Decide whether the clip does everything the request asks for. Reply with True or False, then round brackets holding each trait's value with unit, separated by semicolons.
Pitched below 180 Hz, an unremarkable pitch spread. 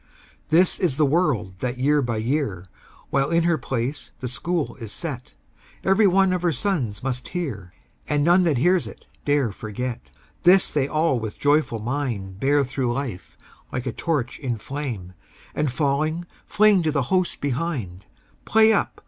False (140 Hz; 5.7 semitones)